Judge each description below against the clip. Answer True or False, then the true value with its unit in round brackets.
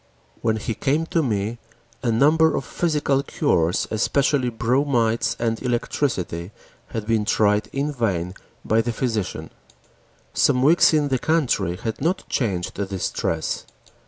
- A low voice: True (115 Hz)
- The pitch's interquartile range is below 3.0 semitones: False (5.1 semitones)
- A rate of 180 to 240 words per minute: False (135 wpm)